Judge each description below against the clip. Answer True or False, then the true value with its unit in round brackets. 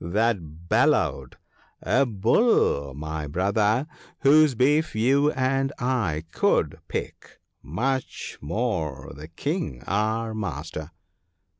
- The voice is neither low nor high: False (110 Hz)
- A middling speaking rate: False (110 wpm)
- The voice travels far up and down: True (8.7 semitones)